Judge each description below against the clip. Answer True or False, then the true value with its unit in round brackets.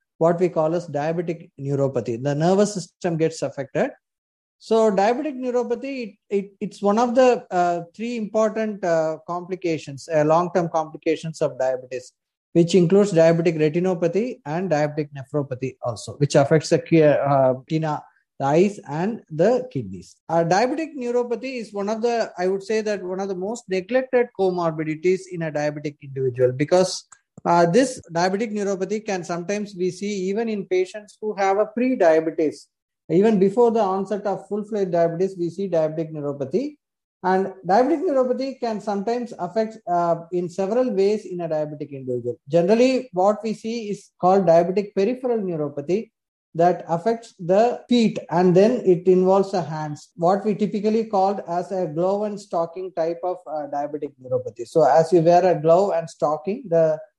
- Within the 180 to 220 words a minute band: False (160 wpm)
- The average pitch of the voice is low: False (185 Hz)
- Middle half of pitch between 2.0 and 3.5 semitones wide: False (4.6 semitones)